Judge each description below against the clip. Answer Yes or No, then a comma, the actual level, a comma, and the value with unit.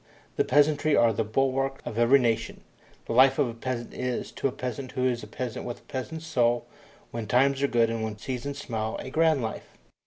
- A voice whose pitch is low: Yes, low, 125 Hz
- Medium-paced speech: No, fast, 215 wpm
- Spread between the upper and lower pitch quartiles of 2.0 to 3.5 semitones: Yes, average, 2.7 semitones